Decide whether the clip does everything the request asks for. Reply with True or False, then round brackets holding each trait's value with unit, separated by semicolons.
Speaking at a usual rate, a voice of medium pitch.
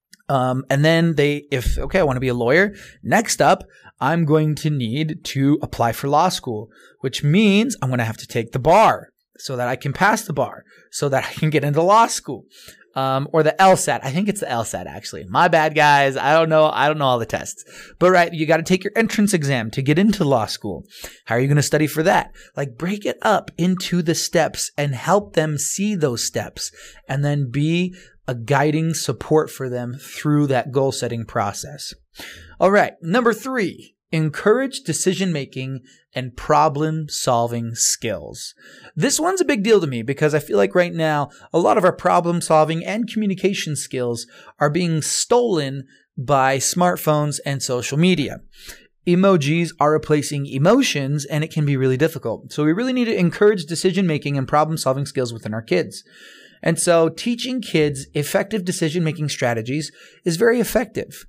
True (190 wpm; 150 Hz)